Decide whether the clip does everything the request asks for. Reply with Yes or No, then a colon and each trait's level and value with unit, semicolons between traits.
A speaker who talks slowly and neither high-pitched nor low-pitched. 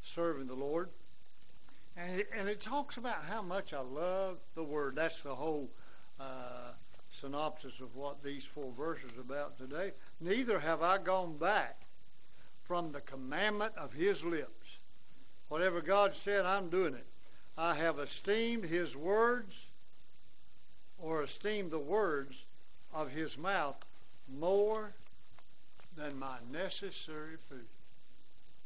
Yes: slow, 125 wpm; medium, 160 Hz